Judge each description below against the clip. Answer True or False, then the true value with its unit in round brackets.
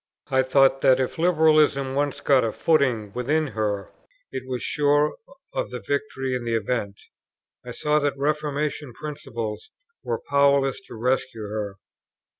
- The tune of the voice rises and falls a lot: False (4.0 semitones)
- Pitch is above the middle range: False (135 Hz)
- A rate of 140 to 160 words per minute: True (145 wpm)